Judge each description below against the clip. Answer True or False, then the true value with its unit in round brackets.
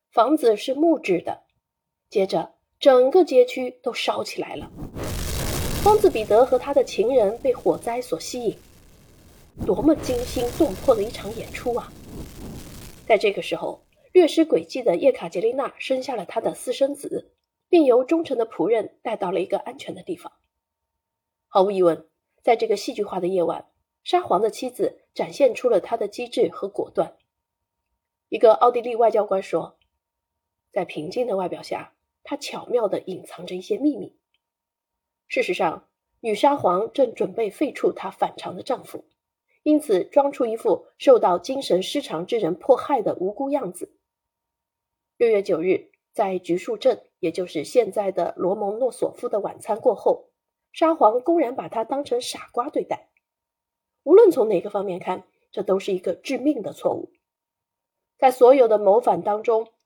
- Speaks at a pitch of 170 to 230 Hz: False (260 Hz)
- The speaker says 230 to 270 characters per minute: True (240 characters per minute)